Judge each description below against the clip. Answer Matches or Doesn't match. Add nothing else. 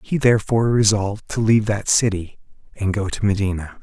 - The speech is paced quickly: Doesn't match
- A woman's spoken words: Doesn't match